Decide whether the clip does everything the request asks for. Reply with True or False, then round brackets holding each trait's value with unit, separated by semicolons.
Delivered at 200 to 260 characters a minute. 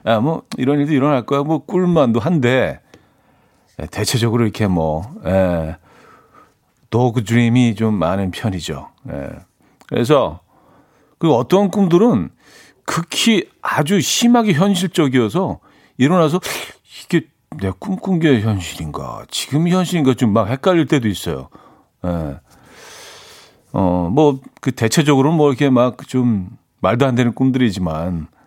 True (240 characters per minute)